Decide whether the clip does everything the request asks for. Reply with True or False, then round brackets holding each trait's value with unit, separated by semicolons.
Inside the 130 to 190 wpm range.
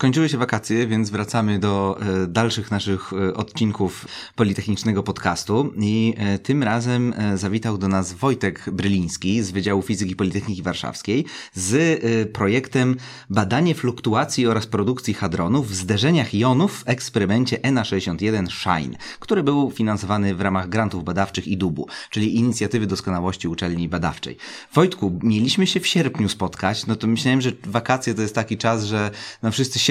True (155 wpm)